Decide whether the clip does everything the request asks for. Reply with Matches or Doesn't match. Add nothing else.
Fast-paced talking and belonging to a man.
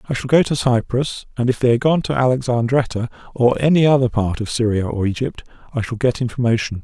Matches